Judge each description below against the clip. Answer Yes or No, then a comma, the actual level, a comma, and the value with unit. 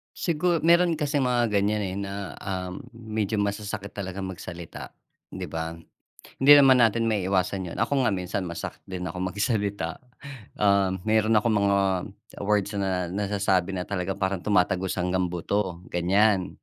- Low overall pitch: Yes, low, 100 Hz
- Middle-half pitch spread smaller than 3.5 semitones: Yes, average, 2.8 semitones